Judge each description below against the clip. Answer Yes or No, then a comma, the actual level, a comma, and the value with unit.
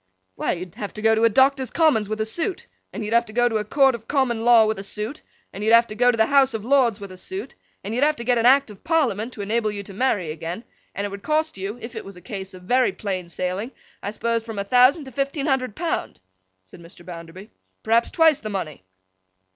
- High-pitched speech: Yes, high, 225 Hz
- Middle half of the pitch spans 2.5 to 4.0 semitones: No, average, 4.5 semitones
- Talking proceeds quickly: Yes, fast, 255 wpm